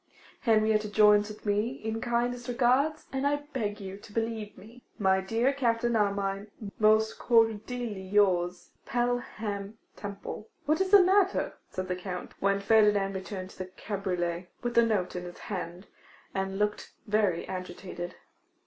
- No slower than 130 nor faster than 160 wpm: Yes, average, 150 wpm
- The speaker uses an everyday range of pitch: Yes, average, 3.5 semitones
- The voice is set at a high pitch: Yes, high, 210 Hz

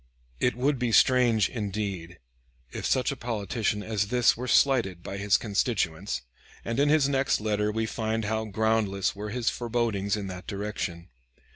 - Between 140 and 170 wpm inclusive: Yes, average, 160 wpm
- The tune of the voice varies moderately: Yes, average, 3.3 semitones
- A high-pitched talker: No, low, 110 Hz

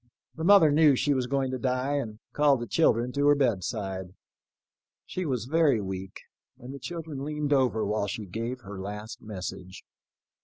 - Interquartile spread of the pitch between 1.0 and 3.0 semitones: No, wide, 5.6 semitones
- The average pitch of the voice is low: Yes, low, 125 Hz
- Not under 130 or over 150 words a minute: No, average, 170 wpm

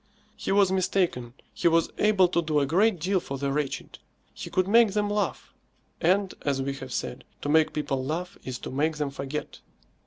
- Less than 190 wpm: No, average, 195 wpm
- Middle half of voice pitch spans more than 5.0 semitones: Yes, wide, 5.5 semitones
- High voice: No, medium, 160 Hz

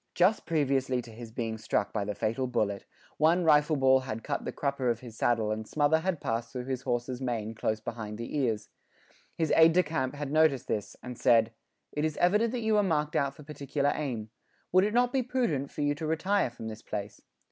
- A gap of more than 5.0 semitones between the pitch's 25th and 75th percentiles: Yes, wide, 5.6 semitones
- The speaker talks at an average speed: No, fast, 220 wpm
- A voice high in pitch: No, low, 135 Hz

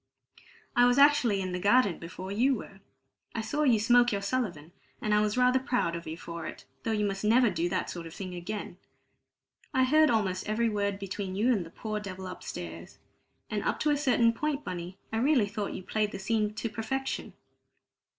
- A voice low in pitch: No, high, 210 Hz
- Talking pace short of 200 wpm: No, fast, 205 wpm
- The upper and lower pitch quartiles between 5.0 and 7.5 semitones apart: No, average, 4.6 semitones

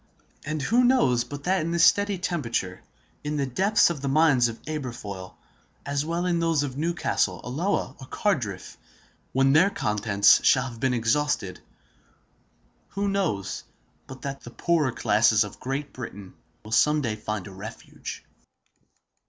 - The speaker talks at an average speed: Yes, average, 150 wpm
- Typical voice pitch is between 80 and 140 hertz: Yes, low, 135 Hz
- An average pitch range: No, wide, 6.5 semitones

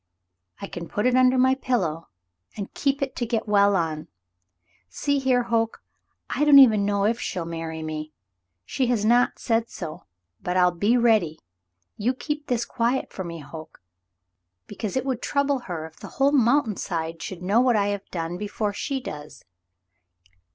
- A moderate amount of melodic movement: No, wide, 6.7 semitones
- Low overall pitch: No, high, 215 Hz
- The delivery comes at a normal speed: Yes, average, 175 wpm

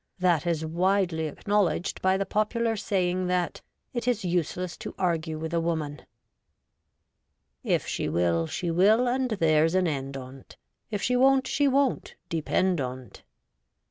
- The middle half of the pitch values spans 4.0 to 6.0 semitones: Yes, average, 4.7 semitones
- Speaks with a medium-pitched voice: Yes, medium, 180 Hz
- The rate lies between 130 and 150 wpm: No, average, 160 wpm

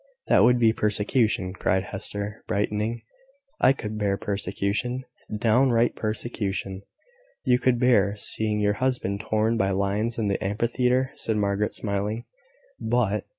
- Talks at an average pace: No, slow, 130 wpm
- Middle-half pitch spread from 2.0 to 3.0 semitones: Yes, average, 2.7 semitones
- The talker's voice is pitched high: No, low, 105 Hz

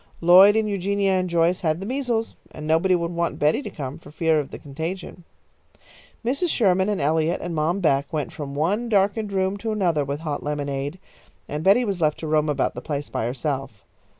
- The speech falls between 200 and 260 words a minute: Yes, fast, 205 wpm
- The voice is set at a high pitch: No, medium, 170 Hz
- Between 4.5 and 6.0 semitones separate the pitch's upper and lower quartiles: Yes, average, 4.8 semitones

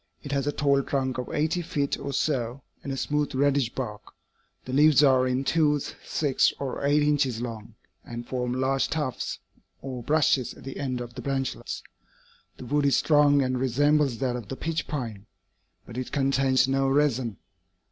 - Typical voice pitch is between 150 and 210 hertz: No, low, 135 Hz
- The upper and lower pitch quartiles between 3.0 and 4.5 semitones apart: No, narrow, 2.4 semitones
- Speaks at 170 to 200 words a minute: Yes, average, 180 wpm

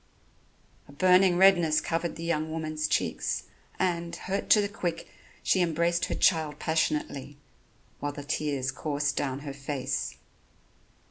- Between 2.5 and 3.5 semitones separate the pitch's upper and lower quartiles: Yes, average, 3.0 semitones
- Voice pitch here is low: No, medium, 160 Hz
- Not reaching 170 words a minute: Yes, slow, 135 wpm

